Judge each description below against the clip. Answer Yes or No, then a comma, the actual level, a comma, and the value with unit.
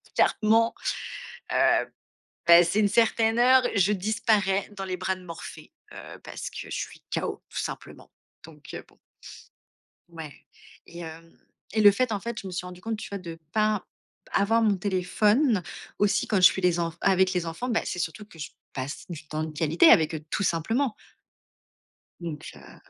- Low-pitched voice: No, high, 190 Hz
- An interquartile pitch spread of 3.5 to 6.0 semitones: Yes, average, 4.3 semitones